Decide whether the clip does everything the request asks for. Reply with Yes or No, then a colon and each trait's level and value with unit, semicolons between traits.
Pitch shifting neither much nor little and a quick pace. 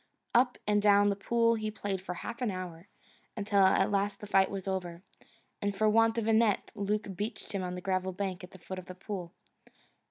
No: narrow, 2.2 semitones; fast, 220 wpm